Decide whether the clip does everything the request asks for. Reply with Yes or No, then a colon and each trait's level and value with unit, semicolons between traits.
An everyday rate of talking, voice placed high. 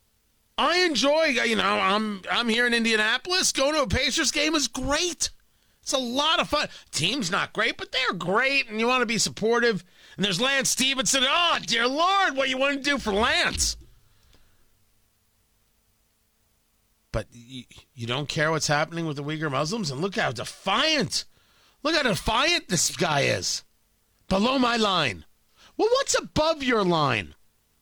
Yes: average, 165 wpm; high, 235 Hz